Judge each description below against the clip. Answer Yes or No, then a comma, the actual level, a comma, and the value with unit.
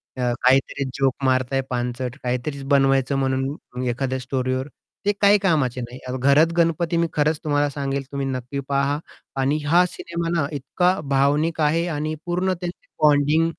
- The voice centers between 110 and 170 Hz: Yes, medium, 140 Hz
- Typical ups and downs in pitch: Yes, average, 3.4 semitones